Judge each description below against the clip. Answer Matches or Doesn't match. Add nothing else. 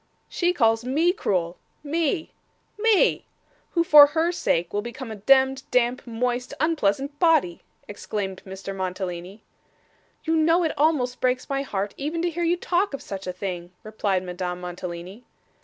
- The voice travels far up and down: Matches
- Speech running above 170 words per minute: Doesn't match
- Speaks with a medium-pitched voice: Doesn't match